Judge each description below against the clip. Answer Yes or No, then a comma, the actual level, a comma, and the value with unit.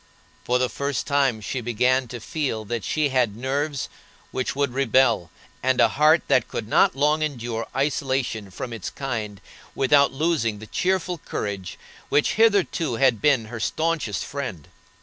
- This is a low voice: Yes, low, 130 Hz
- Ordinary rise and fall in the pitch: Yes, average, 4.1 semitones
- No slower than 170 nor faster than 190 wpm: No, average, 155 wpm